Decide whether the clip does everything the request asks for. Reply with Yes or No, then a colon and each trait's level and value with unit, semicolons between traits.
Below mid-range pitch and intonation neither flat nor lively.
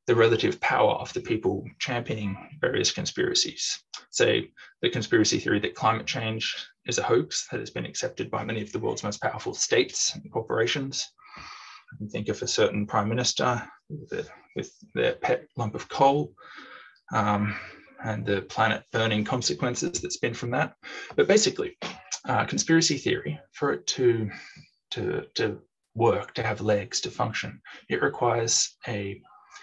No: low, 120 Hz; wide, 7.6 semitones